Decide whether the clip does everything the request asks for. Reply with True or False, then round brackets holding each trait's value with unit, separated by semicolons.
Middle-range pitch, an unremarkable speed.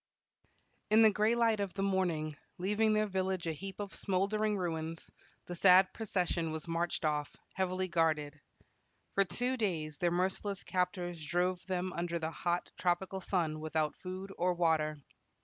True (180 Hz; 155 wpm)